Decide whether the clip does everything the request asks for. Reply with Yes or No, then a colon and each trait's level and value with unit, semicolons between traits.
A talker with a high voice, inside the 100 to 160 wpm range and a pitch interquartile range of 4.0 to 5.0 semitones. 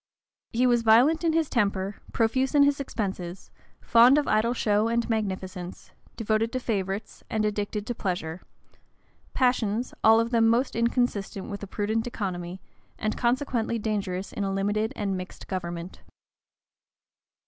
No: high, 220 Hz; average, 150 wpm; average, 3.4 semitones